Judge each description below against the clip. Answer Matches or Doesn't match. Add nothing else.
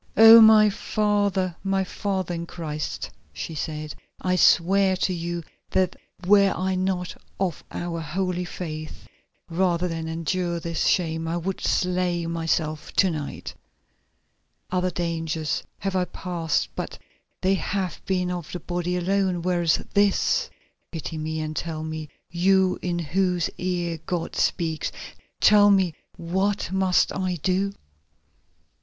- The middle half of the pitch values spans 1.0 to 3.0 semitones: Matches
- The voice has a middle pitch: Matches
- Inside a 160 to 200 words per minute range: Doesn't match